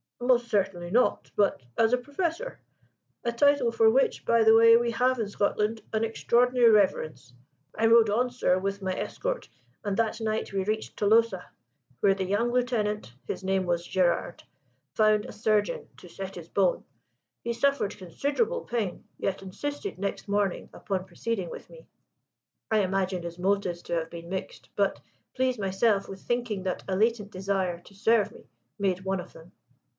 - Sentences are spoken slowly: No, average, 170 wpm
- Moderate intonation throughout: Yes, average, 3.7 semitones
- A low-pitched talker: No, high, 210 Hz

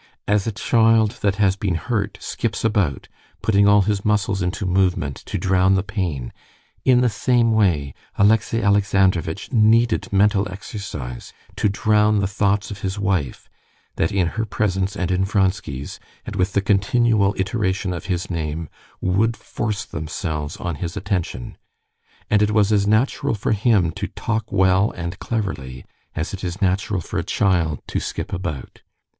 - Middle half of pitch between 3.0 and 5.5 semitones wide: No, narrow, 2.6 semitones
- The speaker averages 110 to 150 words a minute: No, average, 160 wpm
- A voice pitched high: No, low, 100 Hz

